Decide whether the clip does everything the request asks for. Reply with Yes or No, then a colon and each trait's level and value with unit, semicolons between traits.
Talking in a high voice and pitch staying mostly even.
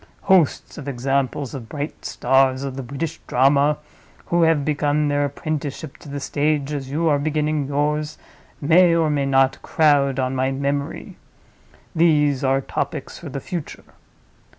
No: medium, 145 Hz; narrow, 1.9 semitones